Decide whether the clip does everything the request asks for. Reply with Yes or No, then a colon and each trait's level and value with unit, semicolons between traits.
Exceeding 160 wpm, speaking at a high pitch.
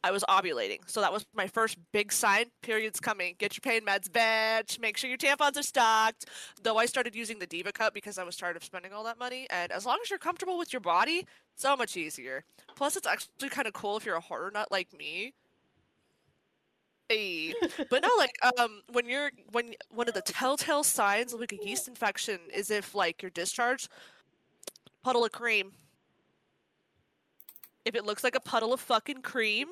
Yes: average, 200 wpm; high, 230 Hz